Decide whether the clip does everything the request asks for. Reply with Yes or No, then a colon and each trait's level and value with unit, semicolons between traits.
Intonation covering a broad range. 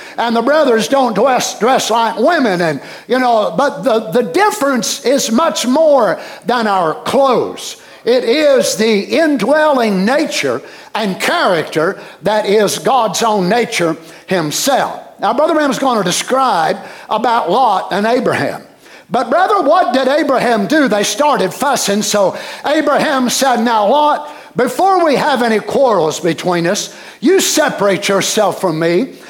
Yes: wide, 6.0 semitones